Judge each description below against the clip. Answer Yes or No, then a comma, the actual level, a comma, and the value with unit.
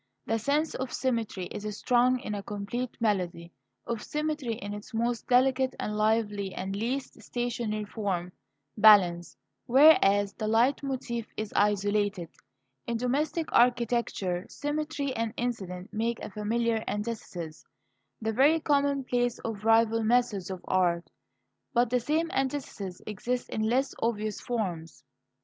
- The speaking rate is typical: No, slow, 130 wpm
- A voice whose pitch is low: No, high, 225 Hz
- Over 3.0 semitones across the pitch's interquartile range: Yes, average, 3.5 semitones